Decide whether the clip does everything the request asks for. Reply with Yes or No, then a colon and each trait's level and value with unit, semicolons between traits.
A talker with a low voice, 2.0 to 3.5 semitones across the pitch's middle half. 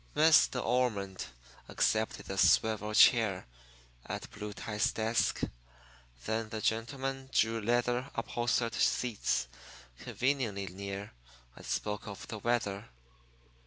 Yes: low, 110 Hz; average, 2.8 semitones